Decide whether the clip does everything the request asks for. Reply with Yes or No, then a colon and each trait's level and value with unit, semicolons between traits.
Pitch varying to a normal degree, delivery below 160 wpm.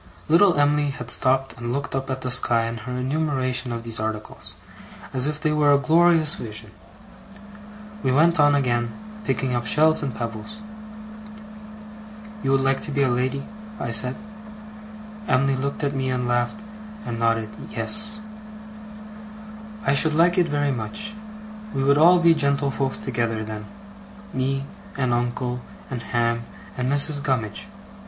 Yes: average, 3.4 semitones; average, 150 wpm